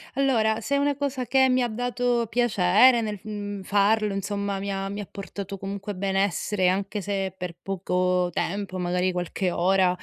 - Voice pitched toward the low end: No, high, 200 Hz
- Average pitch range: Yes, average, 3.0 semitones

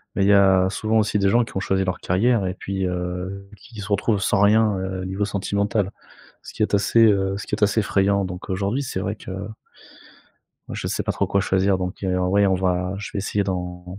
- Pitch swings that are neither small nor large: No, narrow, 1.7 semitones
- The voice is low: Yes, low, 100 Hz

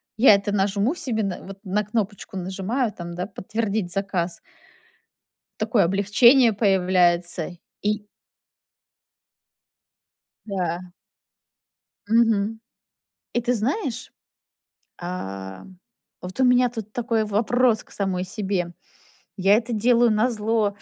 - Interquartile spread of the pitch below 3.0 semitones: No, average, 3.6 semitones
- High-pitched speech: Yes, high, 205 Hz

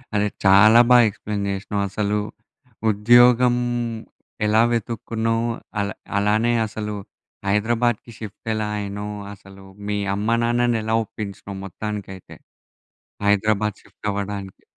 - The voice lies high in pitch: No, low, 105 Hz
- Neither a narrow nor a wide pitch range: No, narrow, 2.1 semitones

